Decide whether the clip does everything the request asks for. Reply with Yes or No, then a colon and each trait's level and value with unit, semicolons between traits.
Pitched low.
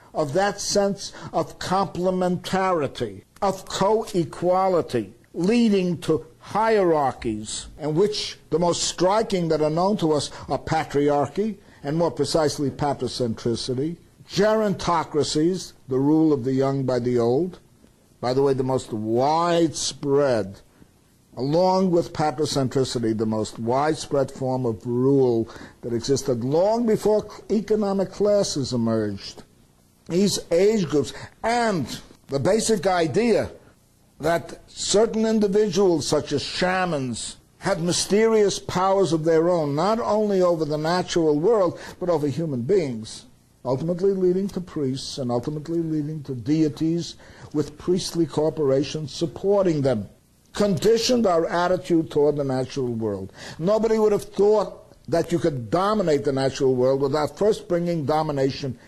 No: medium, 155 Hz